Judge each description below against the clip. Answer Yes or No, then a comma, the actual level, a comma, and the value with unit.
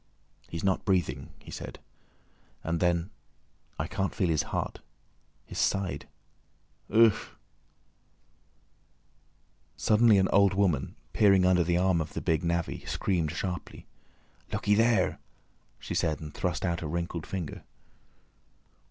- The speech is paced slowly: Yes, slow, 120 wpm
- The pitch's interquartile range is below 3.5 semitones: Yes, average, 2.9 semitones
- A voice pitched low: Yes, very low, 90 Hz